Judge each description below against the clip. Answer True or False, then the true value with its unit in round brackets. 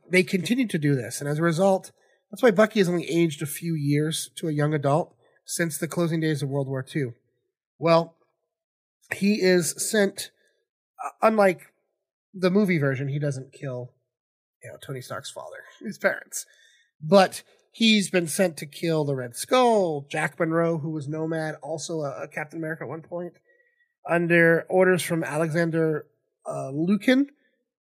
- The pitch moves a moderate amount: True (4.1 semitones)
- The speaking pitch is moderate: True (165 Hz)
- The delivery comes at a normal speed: True (160 wpm)